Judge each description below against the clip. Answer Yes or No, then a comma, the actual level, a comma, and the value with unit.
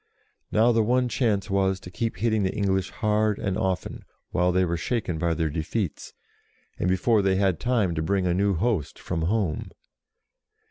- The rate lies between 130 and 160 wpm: No, average, 180 wpm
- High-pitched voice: No, very low, 95 Hz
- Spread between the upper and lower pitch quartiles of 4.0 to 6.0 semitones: No, average, 3.4 semitones